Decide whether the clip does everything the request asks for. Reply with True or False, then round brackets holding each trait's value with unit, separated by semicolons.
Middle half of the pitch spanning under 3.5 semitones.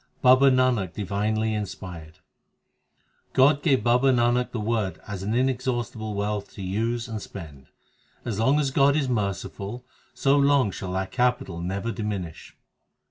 False (4.5 semitones)